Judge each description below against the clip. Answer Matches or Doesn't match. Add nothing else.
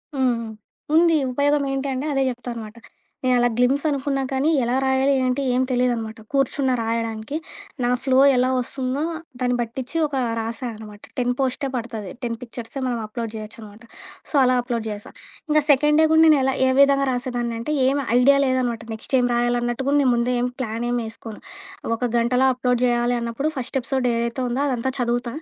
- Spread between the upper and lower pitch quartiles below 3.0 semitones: Matches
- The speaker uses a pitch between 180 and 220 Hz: Doesn't match